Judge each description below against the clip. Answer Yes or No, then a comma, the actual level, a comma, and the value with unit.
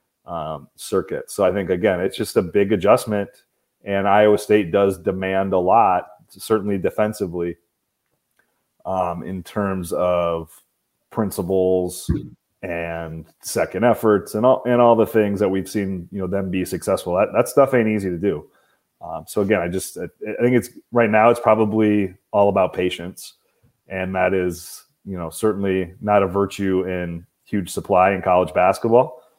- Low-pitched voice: Yes, very low, 95 Hz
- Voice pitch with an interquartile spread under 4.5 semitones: Yes, average, 2.7 semitones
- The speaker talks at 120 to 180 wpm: Yes, average, 160 wpm